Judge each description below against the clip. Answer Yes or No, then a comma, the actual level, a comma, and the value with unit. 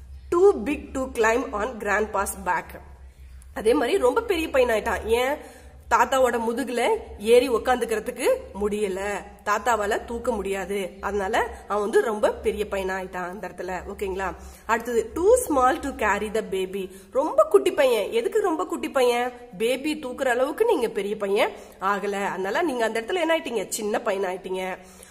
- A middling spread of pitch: No, wide, 6.0 semitones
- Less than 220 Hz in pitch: No, high, 230 Hz